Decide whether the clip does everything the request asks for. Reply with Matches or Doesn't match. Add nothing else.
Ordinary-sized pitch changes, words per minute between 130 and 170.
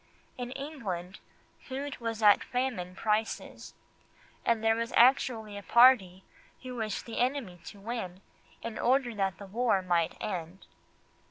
Matches